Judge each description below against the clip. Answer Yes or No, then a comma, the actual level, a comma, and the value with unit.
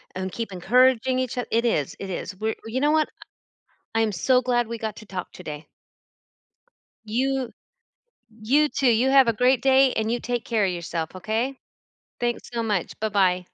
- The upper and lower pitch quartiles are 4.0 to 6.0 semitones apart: Yes, average, 4.4 semitones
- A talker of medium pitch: No, high, 230 Hz